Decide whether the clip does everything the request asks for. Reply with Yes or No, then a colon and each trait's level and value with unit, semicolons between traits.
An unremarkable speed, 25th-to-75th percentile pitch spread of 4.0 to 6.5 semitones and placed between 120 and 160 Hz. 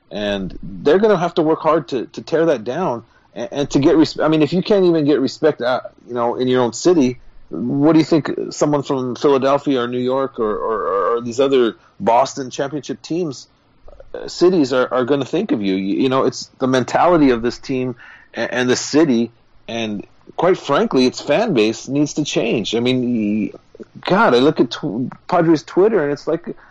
No: fast, 210 wpm; average, 4.5 semitones; low, 135 Hz